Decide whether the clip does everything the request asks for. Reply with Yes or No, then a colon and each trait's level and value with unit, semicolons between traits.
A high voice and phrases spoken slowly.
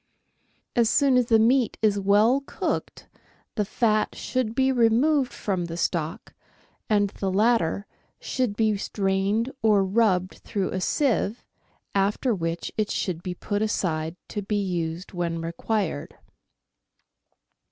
Yes: high, 205 Hz; slow, 130 wpm